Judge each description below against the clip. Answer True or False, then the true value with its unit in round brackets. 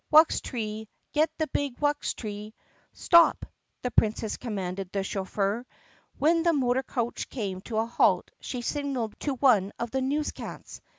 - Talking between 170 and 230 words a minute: False (150 wpm)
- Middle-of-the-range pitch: False (240 Hz)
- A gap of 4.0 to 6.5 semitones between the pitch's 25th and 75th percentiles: True (5.2 semitones)